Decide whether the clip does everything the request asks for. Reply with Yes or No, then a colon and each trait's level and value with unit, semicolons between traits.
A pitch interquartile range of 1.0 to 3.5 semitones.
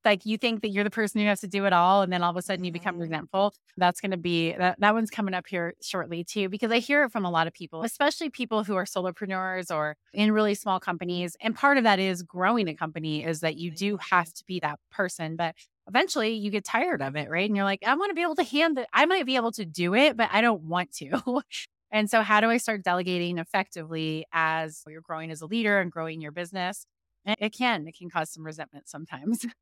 No: average, 4.4 semitones